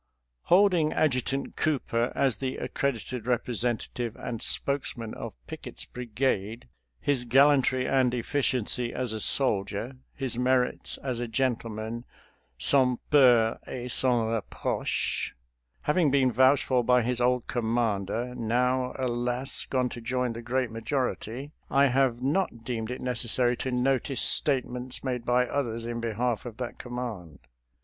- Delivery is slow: No, average, 145 wpm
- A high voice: No, low, 125 Hz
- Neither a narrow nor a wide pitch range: No, narrow, 2.0 semitones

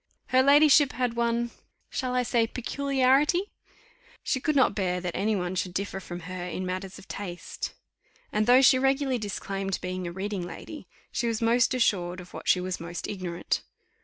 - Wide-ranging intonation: Yes, wide, 5.8 semitones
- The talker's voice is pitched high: Yes, high, 210 Hz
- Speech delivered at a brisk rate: No, average, 180 wpm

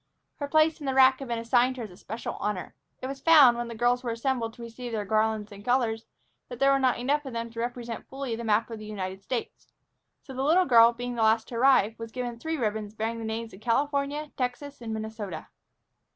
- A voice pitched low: No, high, 235 Hz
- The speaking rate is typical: No, fast, 235 wpm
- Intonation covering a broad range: No, average, 3.0 semitones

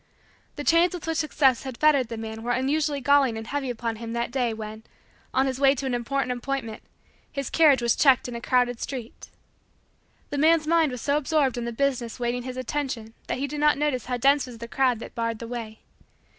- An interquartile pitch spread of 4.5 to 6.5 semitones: No, average, 3.2 semitones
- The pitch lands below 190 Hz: No, very high, 255 Hz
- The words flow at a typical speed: No, fast, 220 wpm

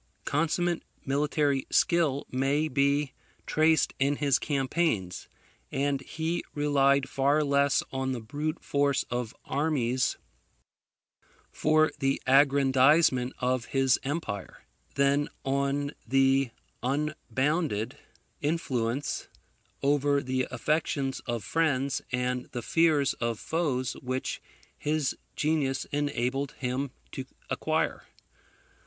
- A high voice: No, medium, 140 Hz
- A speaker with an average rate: No, slow, 100 wpm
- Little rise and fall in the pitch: Yes, narrow, 2.2 semitones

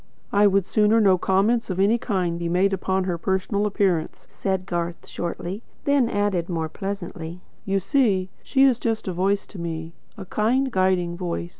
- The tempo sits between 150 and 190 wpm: Yes, average, 175 wpm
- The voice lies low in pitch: No, high, 190 Hz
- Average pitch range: Yes, average, 3.0 semitones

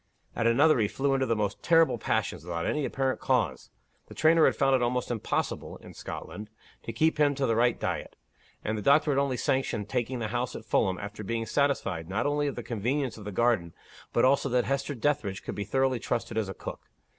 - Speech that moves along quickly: Yes, fast, 225 wpm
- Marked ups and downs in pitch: No, average, 4.2 semitones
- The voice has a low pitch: Yes, low, 120 Hz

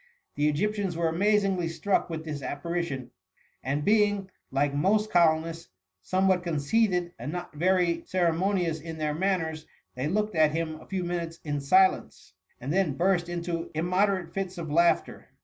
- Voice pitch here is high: No, medium, 170 Hz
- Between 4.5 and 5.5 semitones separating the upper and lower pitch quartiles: No, average, 3.1 semitones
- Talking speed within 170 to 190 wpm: No, average, 150 wpm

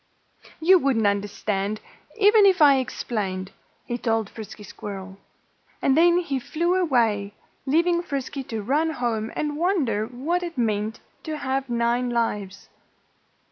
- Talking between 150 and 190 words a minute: No, slow, 135 wpm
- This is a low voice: No, high, 245 Hz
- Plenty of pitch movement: Yes, wide, 6.7 semitones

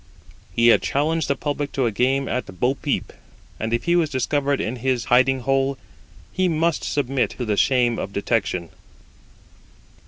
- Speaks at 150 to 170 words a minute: Yes, average, 165 wpm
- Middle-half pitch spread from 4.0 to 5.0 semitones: No, average, 3.3 semitones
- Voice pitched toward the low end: Yes, low, 130 Hz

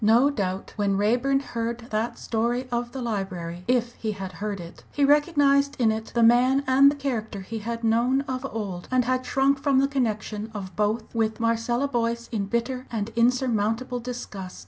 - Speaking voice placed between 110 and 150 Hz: No, high, 235 Hz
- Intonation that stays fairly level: No, average, 3.2 semitones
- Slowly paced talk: No, average, 185 wpm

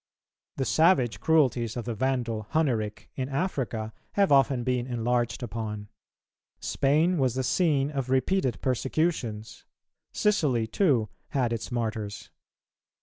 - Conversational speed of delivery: No, slow, 120 wpm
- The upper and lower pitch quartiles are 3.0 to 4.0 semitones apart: Yes, average, 3.7 semitones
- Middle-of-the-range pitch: No, low, 125 Hz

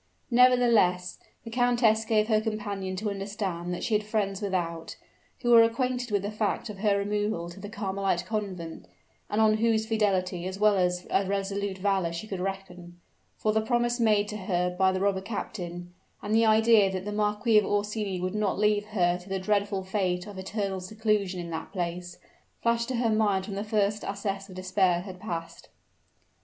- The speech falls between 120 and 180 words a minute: No, average, 190 wpm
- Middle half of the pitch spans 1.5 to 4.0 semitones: Yes, narrow, 2.5 semitones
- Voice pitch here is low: No, high, 200 Hz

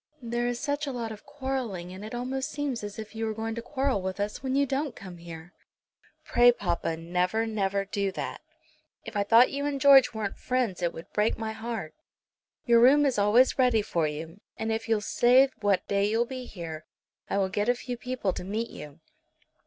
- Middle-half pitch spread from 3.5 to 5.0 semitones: Yes, average, 4.3 semitones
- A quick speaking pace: Yes, fast, 210 wpm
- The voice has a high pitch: Yes, high, 225 Hz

